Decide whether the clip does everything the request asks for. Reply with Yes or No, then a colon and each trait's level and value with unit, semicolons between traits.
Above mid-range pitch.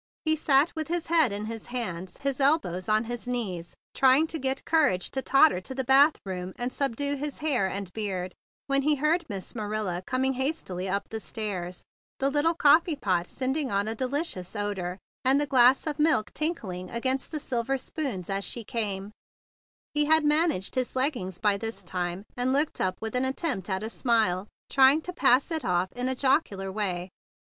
Yes: high, 245 Hz